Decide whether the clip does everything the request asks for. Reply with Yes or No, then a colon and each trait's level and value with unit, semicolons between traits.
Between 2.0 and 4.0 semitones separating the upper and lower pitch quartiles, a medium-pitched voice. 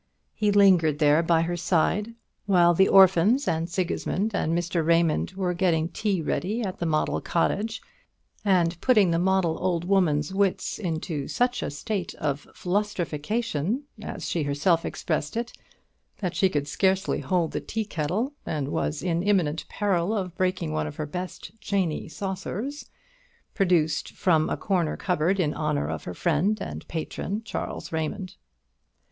Yes: average, 3.7 semitones; medium, 175 Hz